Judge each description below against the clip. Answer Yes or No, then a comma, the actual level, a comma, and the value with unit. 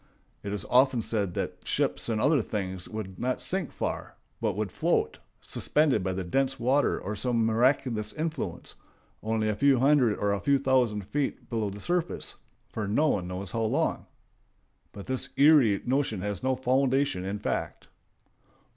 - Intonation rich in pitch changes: No, average, 4.8 semitones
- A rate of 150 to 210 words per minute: Yes, average, 165 wpm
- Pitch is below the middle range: Yes, low, 115 Hz